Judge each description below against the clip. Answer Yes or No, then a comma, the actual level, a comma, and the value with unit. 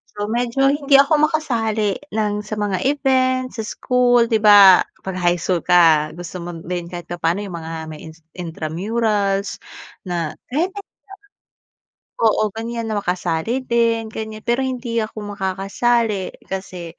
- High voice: Yes, high, 210 Hz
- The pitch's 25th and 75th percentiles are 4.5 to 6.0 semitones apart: Yes, average, 4.8 semitones